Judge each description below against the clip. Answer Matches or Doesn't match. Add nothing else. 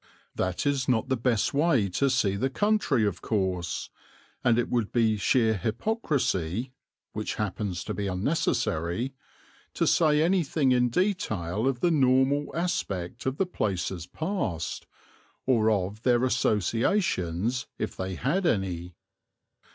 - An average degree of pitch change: Doesn't match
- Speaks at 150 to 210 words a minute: Doesn't match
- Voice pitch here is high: Doesn't match